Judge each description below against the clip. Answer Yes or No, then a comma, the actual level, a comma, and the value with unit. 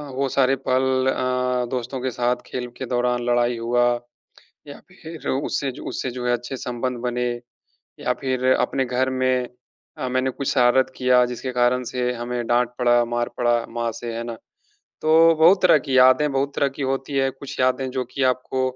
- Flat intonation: Yes, narrow, 1.4 semitones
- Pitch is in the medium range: No, low, 125 Hz